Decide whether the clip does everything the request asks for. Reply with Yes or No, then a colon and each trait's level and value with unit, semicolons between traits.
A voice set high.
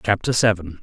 No: low, 100 Hz